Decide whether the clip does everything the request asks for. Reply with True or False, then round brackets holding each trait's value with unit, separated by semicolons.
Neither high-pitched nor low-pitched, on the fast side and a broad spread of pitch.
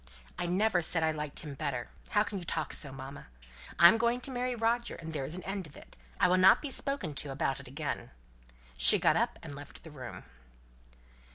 True (165 Hz; 210 wpm; 6.4 semitones)